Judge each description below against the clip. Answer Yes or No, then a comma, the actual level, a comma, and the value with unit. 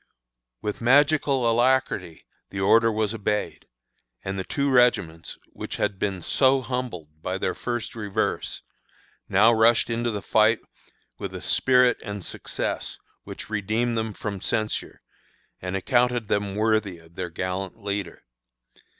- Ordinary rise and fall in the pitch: Yes, average, 3.7 semitones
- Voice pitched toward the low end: Yes, low, 110 Hz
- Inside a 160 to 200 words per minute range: No, slow, 135 wpm